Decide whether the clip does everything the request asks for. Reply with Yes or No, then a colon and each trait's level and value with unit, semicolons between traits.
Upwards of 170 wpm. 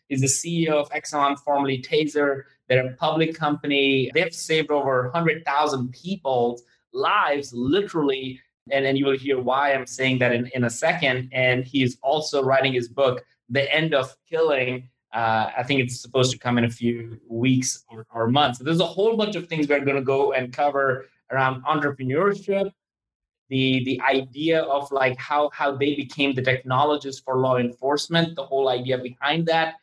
Yes: average, 180 wpm